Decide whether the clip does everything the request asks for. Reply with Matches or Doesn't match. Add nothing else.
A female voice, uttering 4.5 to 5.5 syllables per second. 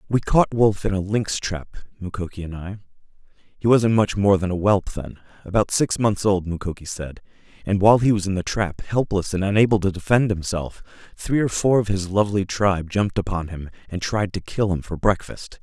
Doesn't match